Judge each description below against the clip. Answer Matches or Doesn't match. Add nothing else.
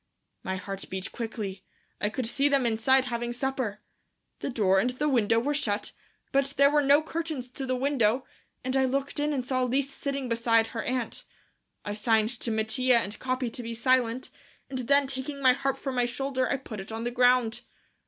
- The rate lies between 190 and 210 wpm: Matches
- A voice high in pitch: Matches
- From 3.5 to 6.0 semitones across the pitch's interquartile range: Doesn't match